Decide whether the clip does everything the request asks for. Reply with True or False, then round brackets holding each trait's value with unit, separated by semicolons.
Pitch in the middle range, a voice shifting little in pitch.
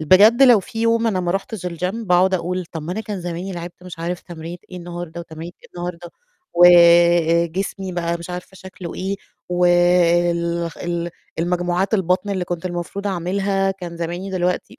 True (175 Hz; 1.7 semitones)